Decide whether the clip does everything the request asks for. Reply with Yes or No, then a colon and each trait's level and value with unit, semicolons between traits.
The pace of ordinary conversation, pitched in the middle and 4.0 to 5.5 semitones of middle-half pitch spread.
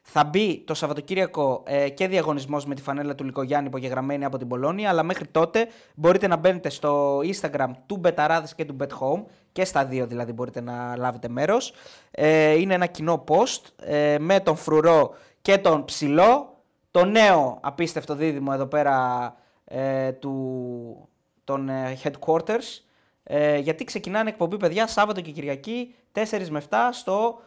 Yes: average, 155 wpm; medium, 155 Hz; average, 5.2 semitones